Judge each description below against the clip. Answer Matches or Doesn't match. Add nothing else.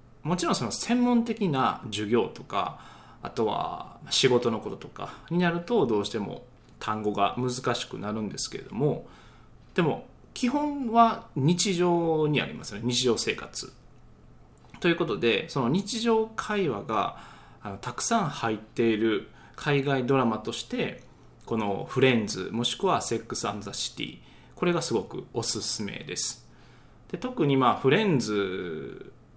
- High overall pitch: Doesn't match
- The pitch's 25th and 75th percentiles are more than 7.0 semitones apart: Matches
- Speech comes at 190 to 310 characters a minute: Matches